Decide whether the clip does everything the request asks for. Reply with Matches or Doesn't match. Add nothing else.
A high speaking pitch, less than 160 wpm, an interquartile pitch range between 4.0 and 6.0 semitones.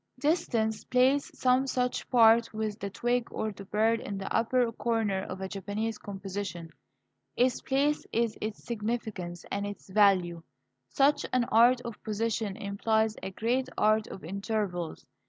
Doesn't match